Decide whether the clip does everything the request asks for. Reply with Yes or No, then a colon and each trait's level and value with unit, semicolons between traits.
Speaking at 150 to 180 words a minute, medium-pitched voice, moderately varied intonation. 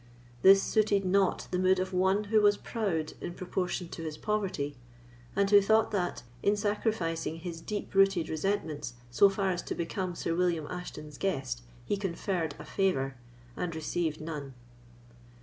Yes: average, 160 wpm; medium, 180 Hz; average, 3.5 semitones